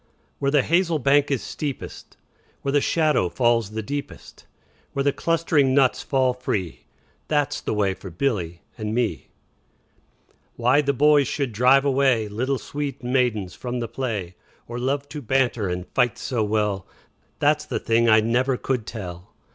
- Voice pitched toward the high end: No, low, 125 Hz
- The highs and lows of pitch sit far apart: No, average, 4.3 semitones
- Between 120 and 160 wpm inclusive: No, average, 170 wpm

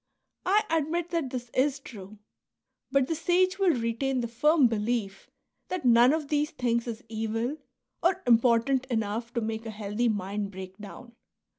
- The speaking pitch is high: Yes, high, 240 Hz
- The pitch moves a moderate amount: Yes, average, 4.9 semitones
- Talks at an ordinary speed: Yes, average, 165 wpm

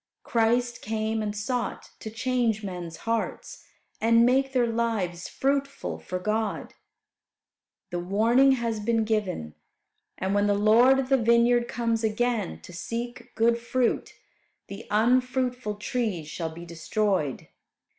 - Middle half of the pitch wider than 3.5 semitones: No, average, 2.9 semitones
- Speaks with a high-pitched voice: Yes, high, 225 Hz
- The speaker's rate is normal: No, slow, 130 wpm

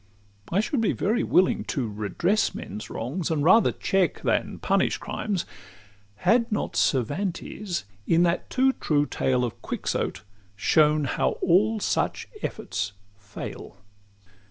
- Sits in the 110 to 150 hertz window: No, medium, 170 Hz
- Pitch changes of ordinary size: No, wide, 8.6 semitones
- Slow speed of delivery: Yes, slow, 130 wpm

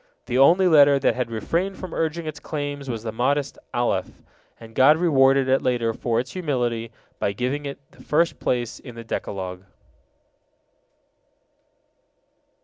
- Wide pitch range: No, average, 4.0 semitones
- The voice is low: Yes, low, 130 Hz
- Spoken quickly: No, average, 145 wpm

